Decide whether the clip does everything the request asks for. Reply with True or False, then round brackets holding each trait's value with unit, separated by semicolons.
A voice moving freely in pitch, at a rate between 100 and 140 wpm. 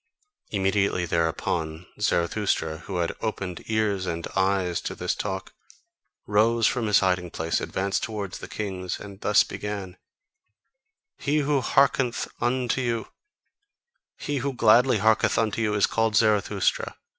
False (3.6 semitones; 135 wpm)